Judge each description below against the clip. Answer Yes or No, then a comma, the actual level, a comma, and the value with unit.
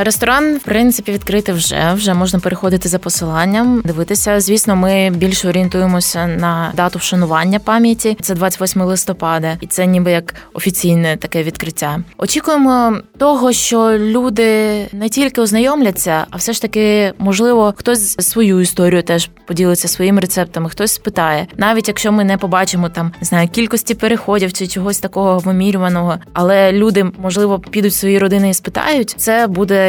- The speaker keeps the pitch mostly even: No, average, 3.4 semitones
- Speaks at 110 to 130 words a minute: No, average, 150 wpm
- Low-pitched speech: No, high, 195 Hz